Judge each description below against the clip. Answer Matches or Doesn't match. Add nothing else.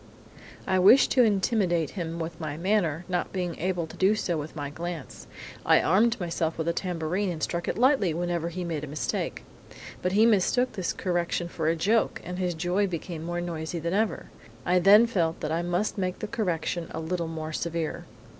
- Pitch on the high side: Doesn't match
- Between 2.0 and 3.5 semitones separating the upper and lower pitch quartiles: Matches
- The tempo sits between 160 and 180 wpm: Doesn't match